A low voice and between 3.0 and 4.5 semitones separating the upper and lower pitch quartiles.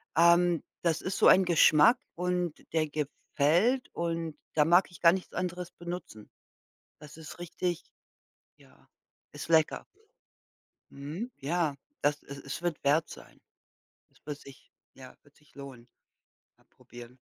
No: medium, 165 Hz; average, 3.3 semitones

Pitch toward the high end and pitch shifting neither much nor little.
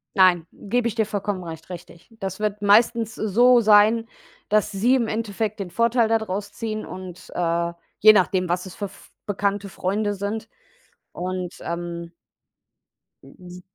Yes: high, 200 Hz; average, 3.2 semitones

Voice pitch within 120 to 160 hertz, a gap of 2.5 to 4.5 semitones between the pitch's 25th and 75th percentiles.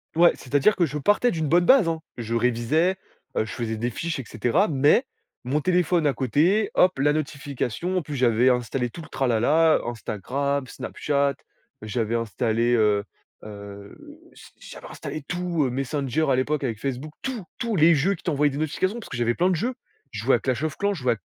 No: medium, 140 Hz; wide, 5.6 semitones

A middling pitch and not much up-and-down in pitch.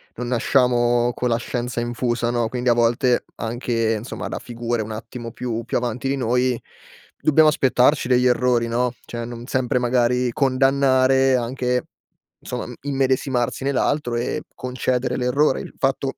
No: low, 125 Hz; narrow, 1.5 semitones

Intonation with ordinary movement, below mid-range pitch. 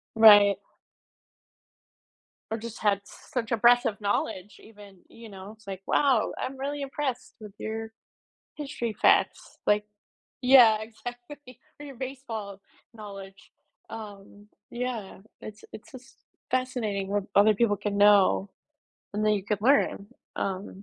No: average, 3.3 semitones; high, 215 Hz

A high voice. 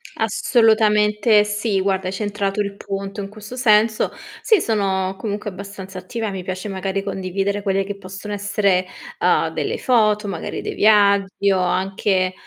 Yes: high, 200 Hz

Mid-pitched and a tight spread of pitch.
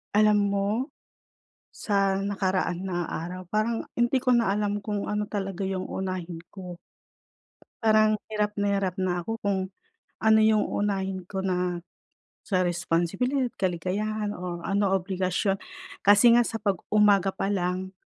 No: high, 195 Hz; narrow, 2.2 semitones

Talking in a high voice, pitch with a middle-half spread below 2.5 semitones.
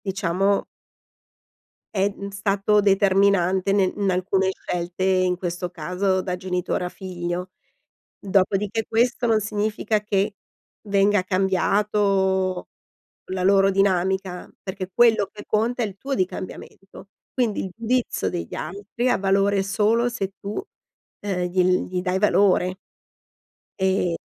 Yes: high, 195 Hz; narrow, 1.8 semitones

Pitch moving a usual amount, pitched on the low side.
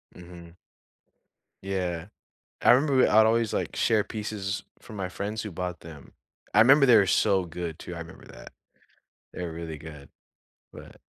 Yes: average, 4.4 semitones; very low, 95 Hz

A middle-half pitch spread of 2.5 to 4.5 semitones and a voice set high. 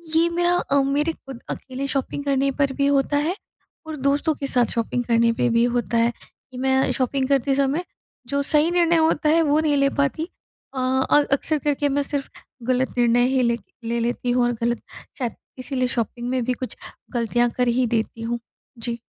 Yes: average, 2.8 semitones; very high, 265 Hz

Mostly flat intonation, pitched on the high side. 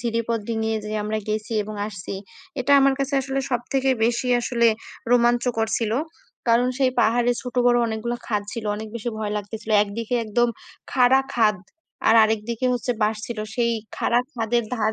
Yes: narrow, 2.0 semitones; high, 230 Hz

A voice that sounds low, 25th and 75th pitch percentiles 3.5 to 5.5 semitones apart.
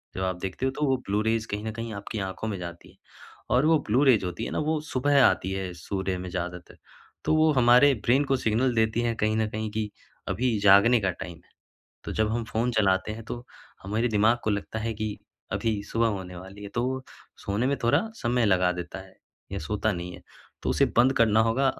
Yes: low, 110 Hz; average, 3.8 semitones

